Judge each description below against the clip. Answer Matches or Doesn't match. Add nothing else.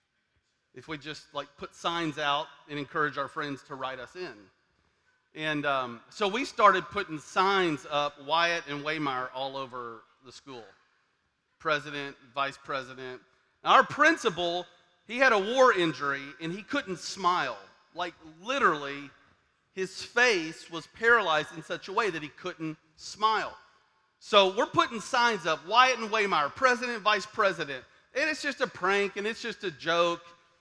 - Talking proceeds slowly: Doesn't match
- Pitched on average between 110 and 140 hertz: Doesn't match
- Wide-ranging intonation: Matches